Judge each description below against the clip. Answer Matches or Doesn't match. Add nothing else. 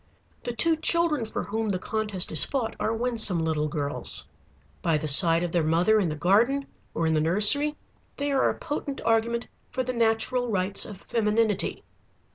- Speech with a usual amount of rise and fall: Doesn't match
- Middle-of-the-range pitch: Doesn't match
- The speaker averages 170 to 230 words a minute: Matches